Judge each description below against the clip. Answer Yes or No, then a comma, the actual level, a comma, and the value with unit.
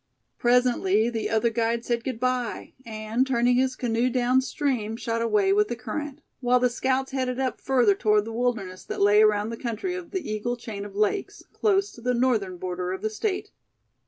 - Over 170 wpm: Yes, average, 195 wpm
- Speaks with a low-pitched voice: No, high, 235 Hz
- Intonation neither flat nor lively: Yes, average, 3.0 semitones